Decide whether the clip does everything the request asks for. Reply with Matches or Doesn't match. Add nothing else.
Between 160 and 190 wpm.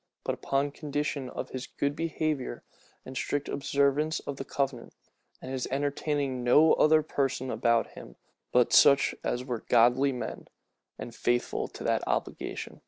Doesn't match